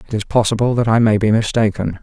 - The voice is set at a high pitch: No, low, 110 Hz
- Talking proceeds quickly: Yes, fast, 235 wpm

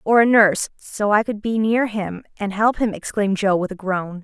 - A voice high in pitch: Yes, high, 205 Hz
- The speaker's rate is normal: No, fast, 240 wpm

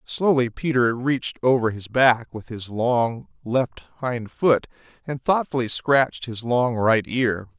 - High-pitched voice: No, low, 120 Hz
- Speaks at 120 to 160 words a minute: Yes, average, 150 wpm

